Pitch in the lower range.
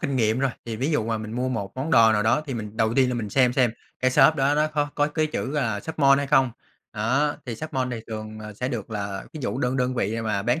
Yes: low, 125 Hz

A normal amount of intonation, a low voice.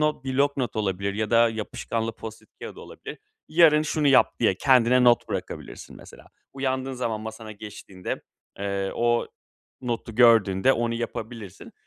Yes: average, 3.3 semitones; low, 115 Hz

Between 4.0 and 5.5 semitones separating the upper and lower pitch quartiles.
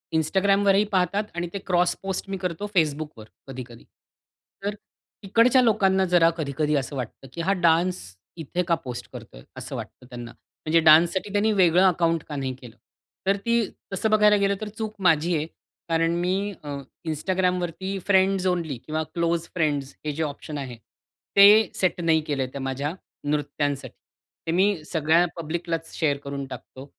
Yes: average, 4.5 semitones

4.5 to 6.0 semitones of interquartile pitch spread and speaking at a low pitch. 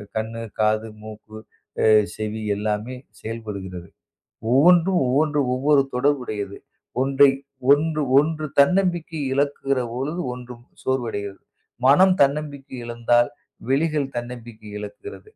Yes: average, 5.2 semitones; low, 130 Hz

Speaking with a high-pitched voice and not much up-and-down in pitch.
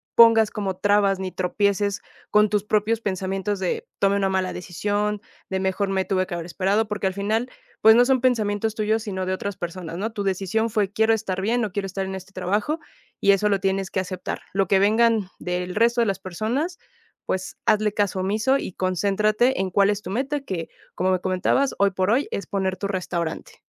Yes: high, 200 Hz; narrow, 2.3 semitones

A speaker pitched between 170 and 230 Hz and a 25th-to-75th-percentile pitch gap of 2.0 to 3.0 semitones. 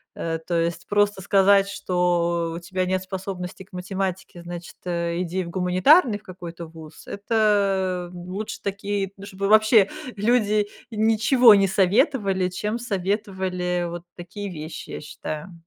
Yes: high, 190 Hz; narrow, 2.6 semitones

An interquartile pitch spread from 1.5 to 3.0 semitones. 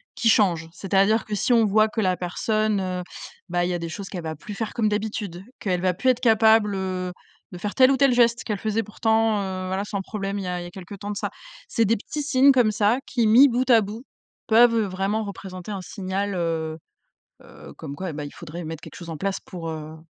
No: average, 3.5 semitones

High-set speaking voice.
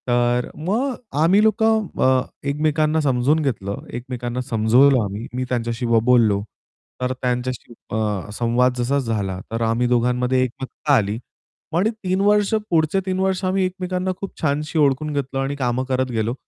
No: low, 130 Hz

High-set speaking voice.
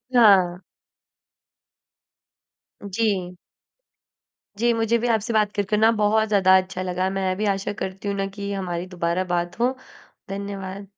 Yes: high, 200 Hz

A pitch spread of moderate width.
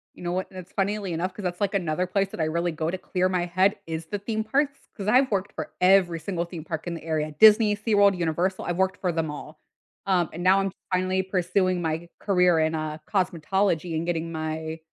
Yes: average, 3.0 semitones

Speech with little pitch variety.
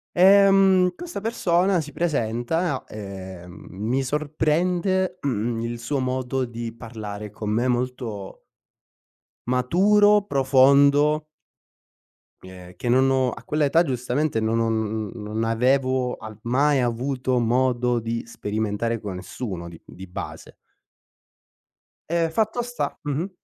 No: average, 5.2 semitones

